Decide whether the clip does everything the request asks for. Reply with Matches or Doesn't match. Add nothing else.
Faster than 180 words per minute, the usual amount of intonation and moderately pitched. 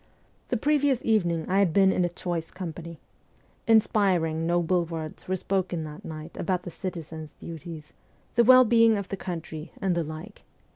Doesn't match